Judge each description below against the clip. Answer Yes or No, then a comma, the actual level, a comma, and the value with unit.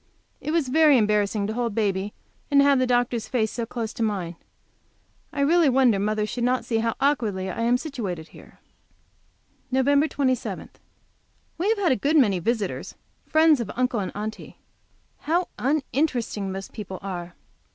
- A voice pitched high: Yes, high, 235 Hz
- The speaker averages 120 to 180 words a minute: Yes, average, 160 wpm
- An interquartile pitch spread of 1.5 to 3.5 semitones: No, average, 5.1 semitones